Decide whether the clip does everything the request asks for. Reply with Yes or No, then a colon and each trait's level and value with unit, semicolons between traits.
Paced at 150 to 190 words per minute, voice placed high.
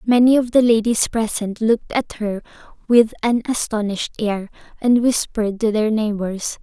Yes: average, 155 wpm; high, 220 Hz